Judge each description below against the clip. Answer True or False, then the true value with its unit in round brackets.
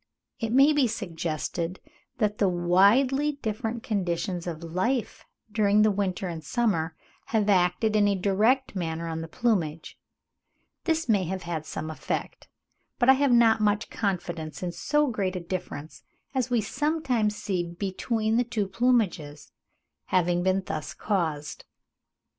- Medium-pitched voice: False (200 Hz)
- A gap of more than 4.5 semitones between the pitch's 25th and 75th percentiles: True (4.9 semitones)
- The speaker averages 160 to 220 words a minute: False (145 wpm)